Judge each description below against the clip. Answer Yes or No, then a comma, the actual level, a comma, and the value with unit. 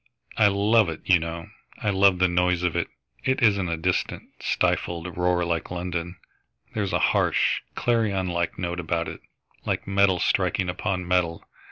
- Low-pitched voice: Yes, very low, 90 Hz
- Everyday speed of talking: Yes, average, 165 wpm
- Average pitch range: No, narrow, 2.2 semitones